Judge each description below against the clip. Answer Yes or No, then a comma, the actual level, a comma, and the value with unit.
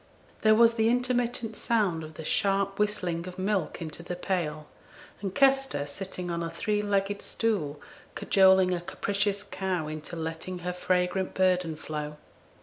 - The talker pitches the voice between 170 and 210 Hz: Yes, medium, 185 Hz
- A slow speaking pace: No, average, 150 wpm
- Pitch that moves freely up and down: No, average, 3.6 semitones